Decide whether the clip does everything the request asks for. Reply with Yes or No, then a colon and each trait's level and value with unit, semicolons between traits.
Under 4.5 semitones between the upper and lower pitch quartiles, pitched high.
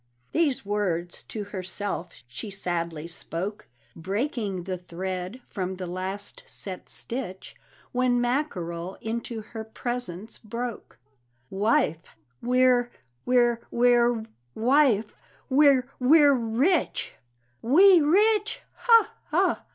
No: average, 5.3 semitones; high, 225 Hz